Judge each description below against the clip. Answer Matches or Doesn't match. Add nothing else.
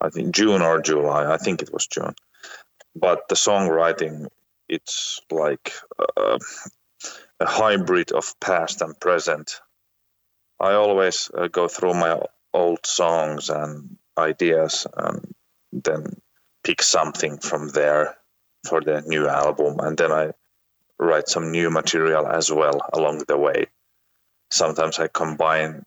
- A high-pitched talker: Doesn't match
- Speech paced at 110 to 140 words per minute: Matches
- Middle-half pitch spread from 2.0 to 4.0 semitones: Matches